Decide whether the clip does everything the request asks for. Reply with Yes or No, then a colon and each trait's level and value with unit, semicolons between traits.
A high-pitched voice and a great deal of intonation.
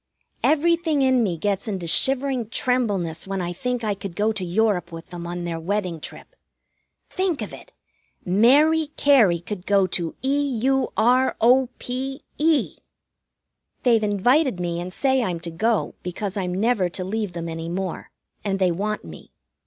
Yes: high, 210 Hz; wide, 6.5 semitones